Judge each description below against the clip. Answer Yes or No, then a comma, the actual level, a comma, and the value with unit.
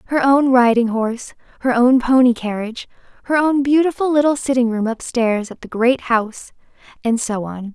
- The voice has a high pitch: Yes, high, 245 Hz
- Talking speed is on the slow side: No, average, 170 wpm